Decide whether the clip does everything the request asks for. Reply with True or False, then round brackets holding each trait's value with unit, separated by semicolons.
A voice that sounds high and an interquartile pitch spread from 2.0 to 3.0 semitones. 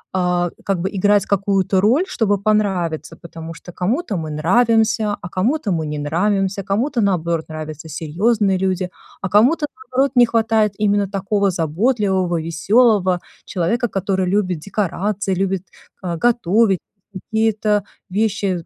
False (195 Hz; 3.4 semitones)